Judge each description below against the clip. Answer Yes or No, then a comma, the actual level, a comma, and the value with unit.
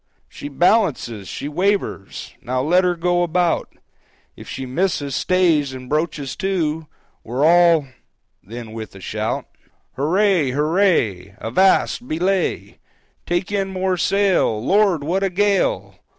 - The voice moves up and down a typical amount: No, wide, 6.0 semitones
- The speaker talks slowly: Yes, slow, 120 wpm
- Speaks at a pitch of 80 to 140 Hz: No, medium, 170 Hz